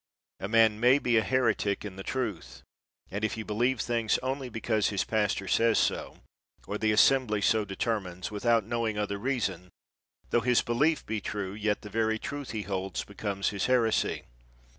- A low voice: Yes, low, 110 Hz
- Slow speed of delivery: No, average, 175 wpm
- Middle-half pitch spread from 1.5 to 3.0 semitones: Yes, average, 2.7 semitones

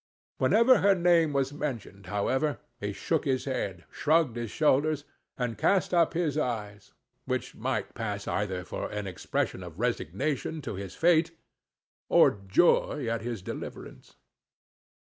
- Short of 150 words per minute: Yes, average, 140 wpm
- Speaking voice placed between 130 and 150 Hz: Yes, low, 135 Hz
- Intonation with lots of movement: Yes, wide, 7.2 semitones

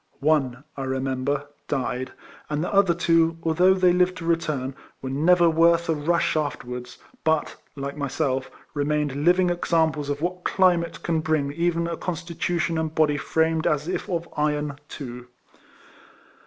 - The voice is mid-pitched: Yes, medium, 160 Hz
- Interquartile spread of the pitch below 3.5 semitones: Yes, average, 3.1 semitones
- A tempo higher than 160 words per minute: No, average, 150 wpm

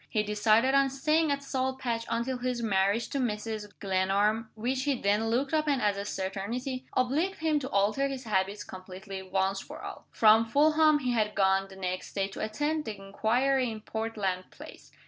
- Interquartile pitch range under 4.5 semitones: No, average, 4.9 semitones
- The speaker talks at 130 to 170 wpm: No, average, 185 wpm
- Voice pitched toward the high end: Yes, high, 225 Hz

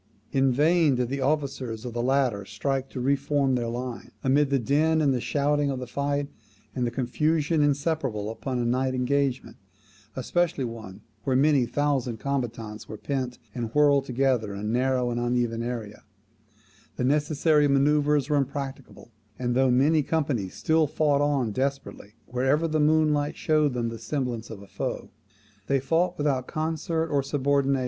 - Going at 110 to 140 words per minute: No, average, 155 wpm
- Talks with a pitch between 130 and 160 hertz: Yes, low, 135 Hz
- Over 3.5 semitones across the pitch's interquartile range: No, average, 3.0 semitones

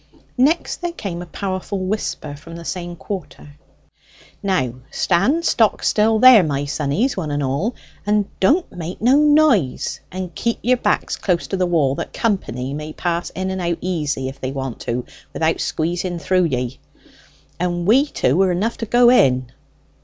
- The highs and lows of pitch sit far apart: Yes, wide, 6.3 semitones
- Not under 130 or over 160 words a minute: No, average, 170 wpm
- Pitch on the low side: No, medium, 180 Hz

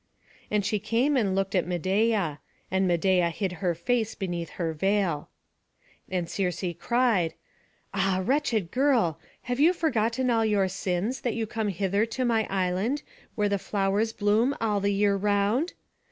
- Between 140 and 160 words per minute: Yes, average, 155 wpm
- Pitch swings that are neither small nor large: Yes, average, 3.5 semitones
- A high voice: Yes, high, 205 Hz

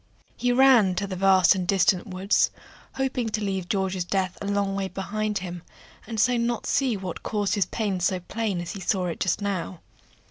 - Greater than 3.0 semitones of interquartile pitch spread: No, narrow, 2.5 semitones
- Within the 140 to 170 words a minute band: No, average, 200 wpm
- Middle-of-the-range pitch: No, high, 195 Hz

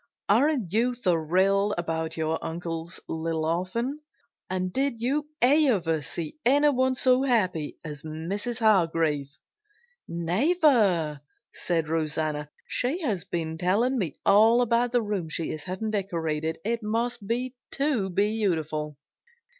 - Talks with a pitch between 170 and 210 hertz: Yes, high, 190 Hz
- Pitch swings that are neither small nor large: No, wide, 6.8 semitones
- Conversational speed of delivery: No, slow, 125 wpm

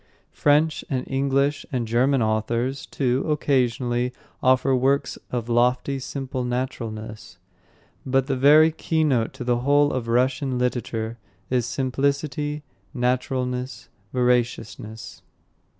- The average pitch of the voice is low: Yes, low, 130 Hz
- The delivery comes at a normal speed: No, slow, 105 wpm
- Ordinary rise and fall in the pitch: No, narrow, 2.2 semitones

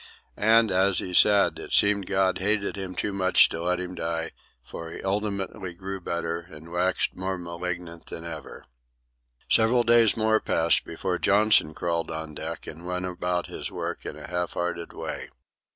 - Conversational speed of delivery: Yes, average, 170 wpm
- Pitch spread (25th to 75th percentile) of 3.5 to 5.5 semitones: No, average, 2.7 semitones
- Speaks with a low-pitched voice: Yes, very low, 90 Hz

